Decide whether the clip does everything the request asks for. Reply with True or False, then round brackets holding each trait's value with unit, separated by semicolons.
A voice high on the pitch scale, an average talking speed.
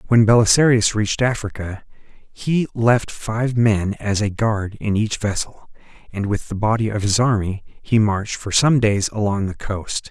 False (110 Hz; 170 wpm)